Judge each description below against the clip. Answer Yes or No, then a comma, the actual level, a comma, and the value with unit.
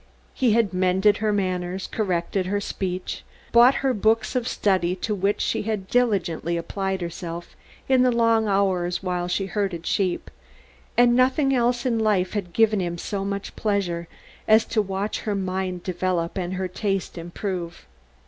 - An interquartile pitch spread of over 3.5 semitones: No, average, 3.2 semitones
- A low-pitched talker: No, high, 195 Hz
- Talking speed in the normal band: Yes, average, 160 wpm